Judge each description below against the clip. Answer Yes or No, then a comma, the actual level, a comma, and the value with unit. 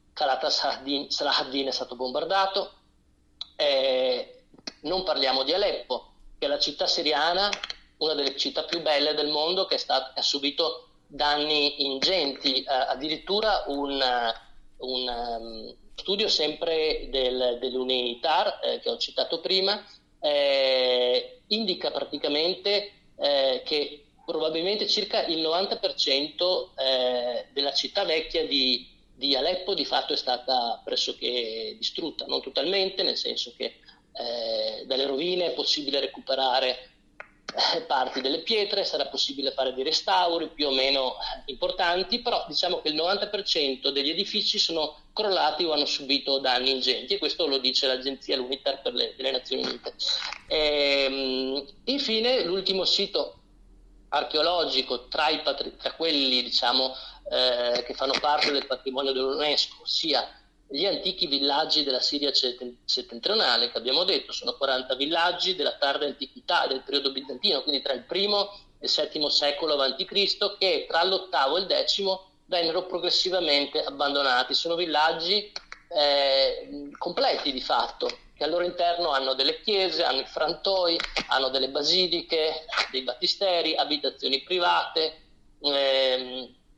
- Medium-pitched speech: Yes, medium, 150 Hz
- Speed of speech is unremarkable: Yes, average, 135 wpm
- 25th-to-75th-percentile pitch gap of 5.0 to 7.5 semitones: Yes, wide, 5.6 semitones